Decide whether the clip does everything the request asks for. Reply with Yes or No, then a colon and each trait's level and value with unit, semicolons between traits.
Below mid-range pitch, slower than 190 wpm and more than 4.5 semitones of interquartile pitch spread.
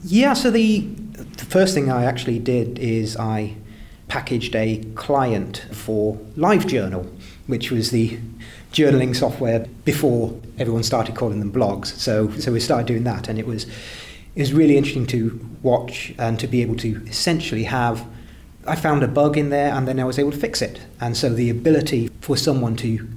No: low, 120 Hz; average, 180 wpm; average, 3.6 semitones